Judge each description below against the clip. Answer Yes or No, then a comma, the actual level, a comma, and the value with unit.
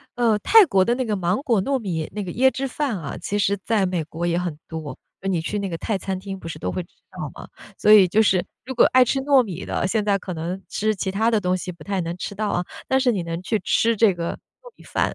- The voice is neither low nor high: No, high, 195 Hz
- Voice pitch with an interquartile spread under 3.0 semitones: No, average, 4.3 semitones